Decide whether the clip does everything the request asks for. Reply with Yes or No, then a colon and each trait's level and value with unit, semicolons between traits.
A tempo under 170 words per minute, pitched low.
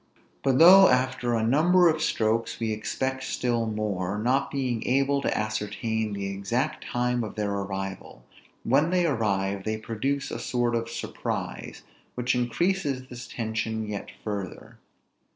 Yes: average, 145 wpm; low, 115 Hz